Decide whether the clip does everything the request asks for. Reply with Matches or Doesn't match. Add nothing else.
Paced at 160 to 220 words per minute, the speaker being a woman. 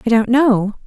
Matches